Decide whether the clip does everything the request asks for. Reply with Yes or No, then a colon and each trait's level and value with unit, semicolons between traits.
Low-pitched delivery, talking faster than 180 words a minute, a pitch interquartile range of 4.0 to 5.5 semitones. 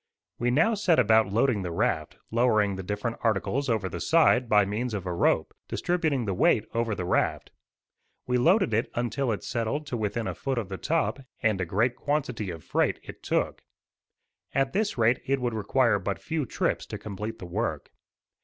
Yes: low, 115 Hz; average, 190 wpm; average, 4.5 semitones